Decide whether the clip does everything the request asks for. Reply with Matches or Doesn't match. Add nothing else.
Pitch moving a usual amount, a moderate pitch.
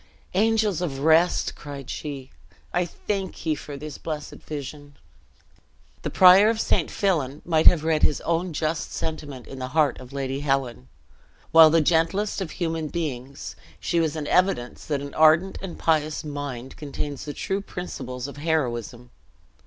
Matches